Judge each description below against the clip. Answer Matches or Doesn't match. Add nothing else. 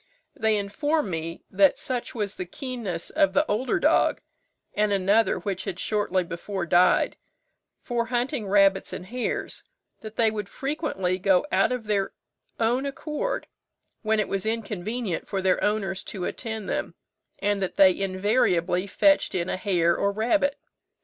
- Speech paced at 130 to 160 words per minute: Matches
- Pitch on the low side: Doesn't match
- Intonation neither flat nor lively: Matches